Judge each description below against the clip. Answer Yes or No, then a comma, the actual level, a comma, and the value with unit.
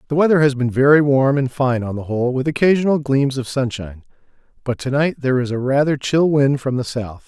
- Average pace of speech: No, fast, 230 wpm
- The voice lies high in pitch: No, low, 135 Hz